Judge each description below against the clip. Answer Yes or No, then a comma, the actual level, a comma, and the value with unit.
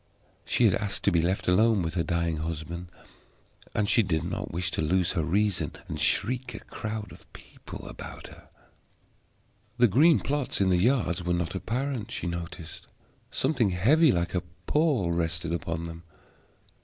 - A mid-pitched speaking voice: No, very low, 90 Hz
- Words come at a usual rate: Yes, average, 165 wpm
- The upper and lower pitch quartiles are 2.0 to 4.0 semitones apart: No, average, 4.9 semitones